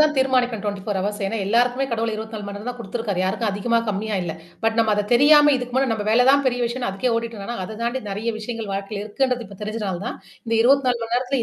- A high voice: Yes, high, 230 Hz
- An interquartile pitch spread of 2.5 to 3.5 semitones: Yes, average, 3.2 semitones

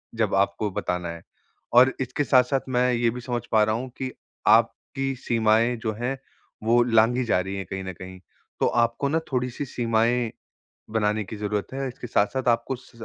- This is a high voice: No, low, 115 Hz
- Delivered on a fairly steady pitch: No, average, 3.0 semitones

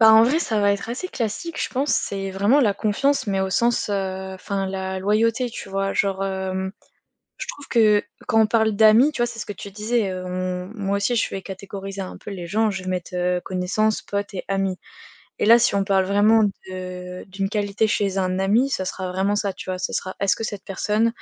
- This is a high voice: Yes, high, 200 Hz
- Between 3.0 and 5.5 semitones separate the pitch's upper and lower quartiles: No, narrow, 2.6 semitones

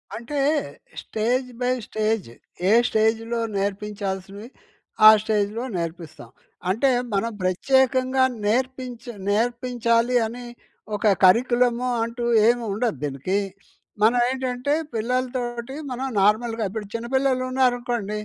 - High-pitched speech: Yes, high, 235 Hz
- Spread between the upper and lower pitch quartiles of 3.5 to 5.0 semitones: No, average, 3.0 semitones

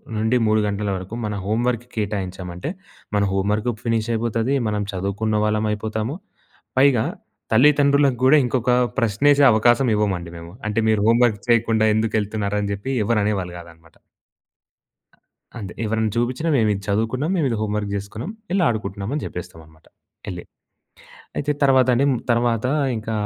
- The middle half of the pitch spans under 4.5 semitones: Yes, average, 2.9 semitones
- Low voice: Yes, low, 110 Hz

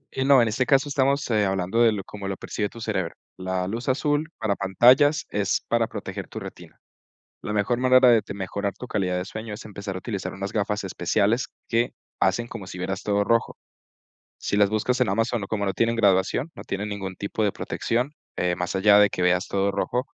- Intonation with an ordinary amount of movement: Yes, average, 3.4 semitones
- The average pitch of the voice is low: Yes, low, 105 Hz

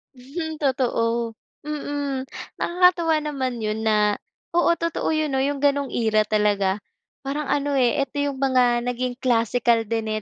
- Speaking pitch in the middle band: No, very high, 260 Hz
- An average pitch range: Yes, average, 4.0 semitones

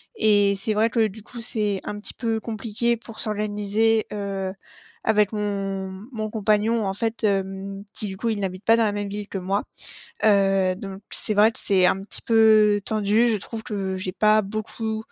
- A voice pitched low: No, high, 210 Hz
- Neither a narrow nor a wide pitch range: No, narrow, 1.9 semitones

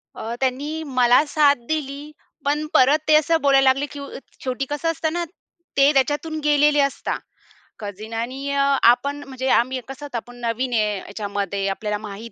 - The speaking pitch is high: Yes, very high, 270 Hz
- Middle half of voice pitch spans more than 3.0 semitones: Yes, average, 3.9 semitones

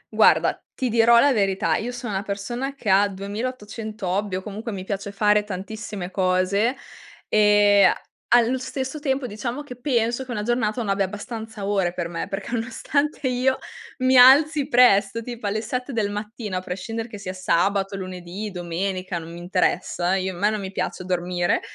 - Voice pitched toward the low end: No, high, 210 Hz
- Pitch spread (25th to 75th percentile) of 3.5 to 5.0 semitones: Yes, average, 4.0 semitones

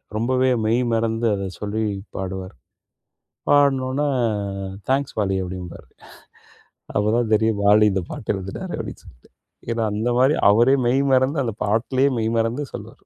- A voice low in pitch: Yes, low, 115 Hz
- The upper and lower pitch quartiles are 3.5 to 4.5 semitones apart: Yes, average, 4.1 semitones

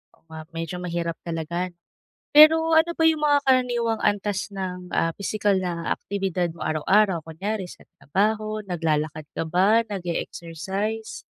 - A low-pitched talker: No, high, 190 Hz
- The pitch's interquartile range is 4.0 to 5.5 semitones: Yes, average, 4.3 semitones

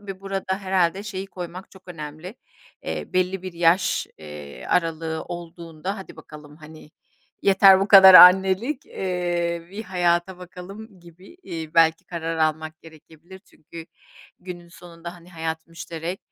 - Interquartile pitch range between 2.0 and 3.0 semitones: Yes, narrow, 2.6 semitones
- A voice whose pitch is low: No, medium, 175 Hz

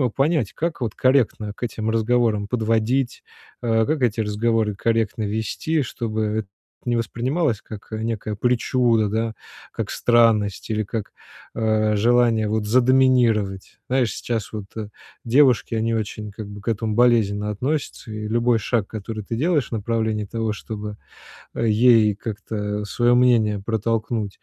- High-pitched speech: No, low, 110 Hz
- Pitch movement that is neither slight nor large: No, narrow, 2.2 semitones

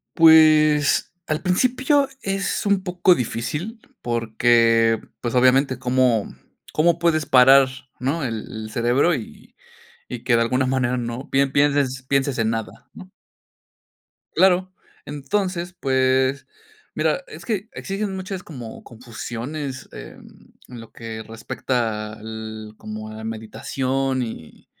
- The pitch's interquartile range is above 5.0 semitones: Yes, wide, 5.6 semitones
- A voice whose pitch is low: Yes, low, 130 Hz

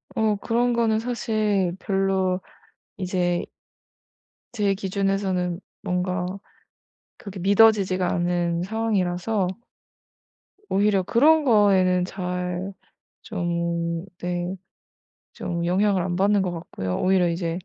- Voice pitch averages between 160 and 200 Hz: Yes, medium, 185 Hz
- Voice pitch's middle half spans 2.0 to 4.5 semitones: Yes, average, 2.7 semitones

